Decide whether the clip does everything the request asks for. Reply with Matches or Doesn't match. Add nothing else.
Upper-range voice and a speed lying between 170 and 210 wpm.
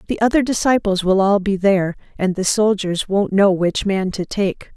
Matches